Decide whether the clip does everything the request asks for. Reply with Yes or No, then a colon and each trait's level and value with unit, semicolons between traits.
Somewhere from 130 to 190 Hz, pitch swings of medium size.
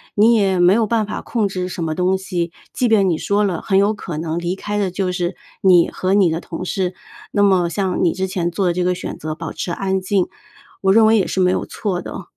No: medium, 185 Hz; narrow, 2.3 semitones